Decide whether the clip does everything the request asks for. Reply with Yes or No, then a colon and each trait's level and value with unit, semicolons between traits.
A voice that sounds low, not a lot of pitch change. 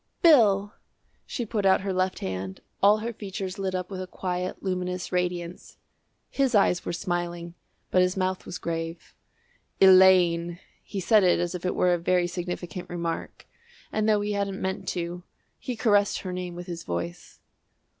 No: medium, 185 Hz; narrow, 2.1 semitones